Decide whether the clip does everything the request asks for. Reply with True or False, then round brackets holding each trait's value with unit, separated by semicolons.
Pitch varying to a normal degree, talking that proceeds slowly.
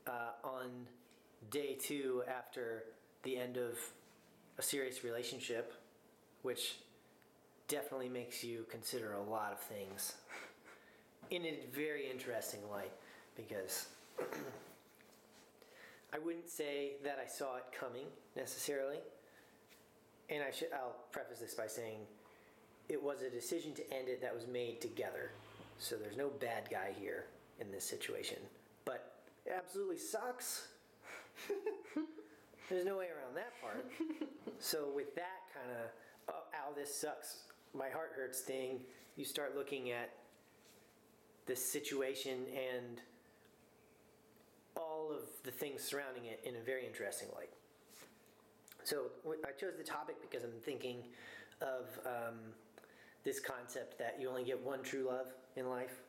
False (7.4 semitones; 130 wpm)